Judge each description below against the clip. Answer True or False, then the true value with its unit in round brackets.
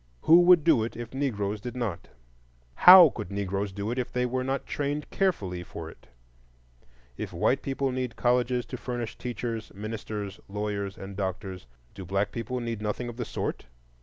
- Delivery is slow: False (175 wpm)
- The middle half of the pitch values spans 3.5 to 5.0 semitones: True (4.0 semitones)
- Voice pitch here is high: False (115 Hz)